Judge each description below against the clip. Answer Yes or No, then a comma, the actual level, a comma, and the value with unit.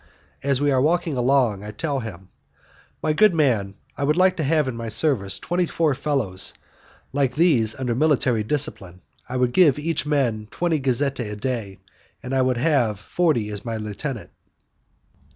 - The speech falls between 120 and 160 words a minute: No, average, 170 wpm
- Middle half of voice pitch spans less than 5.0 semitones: No, average, 5.3 semitones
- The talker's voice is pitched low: Yes, low, 130 Hz